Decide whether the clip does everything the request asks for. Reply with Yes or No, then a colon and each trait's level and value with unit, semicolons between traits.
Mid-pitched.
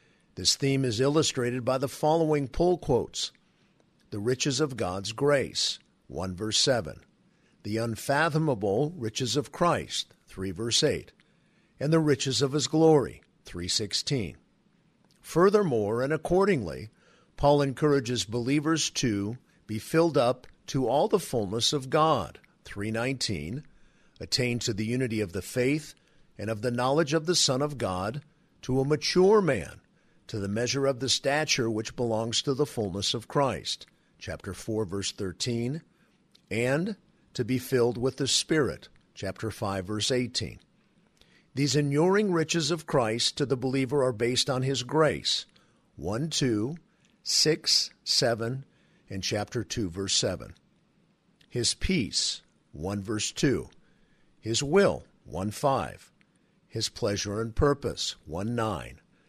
No: low, 130 Hz